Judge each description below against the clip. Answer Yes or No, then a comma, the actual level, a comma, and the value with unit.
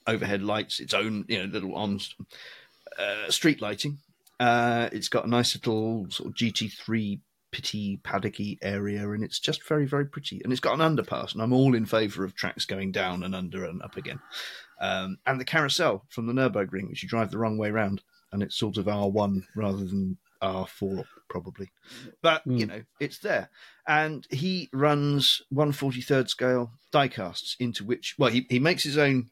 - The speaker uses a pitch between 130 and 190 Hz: No, low, 110 Hz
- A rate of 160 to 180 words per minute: No, average, 200 wpm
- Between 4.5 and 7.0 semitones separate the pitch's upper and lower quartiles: Yes, average, 4.8 semitones